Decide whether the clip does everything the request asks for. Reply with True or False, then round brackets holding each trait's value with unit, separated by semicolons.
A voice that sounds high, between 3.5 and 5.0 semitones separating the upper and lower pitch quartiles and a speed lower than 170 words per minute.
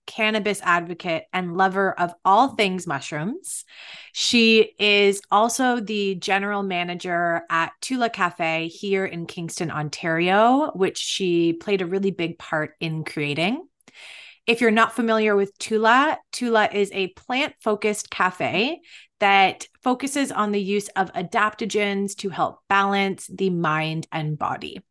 True (195 Hz; 4.1 semitones; 135 wpm)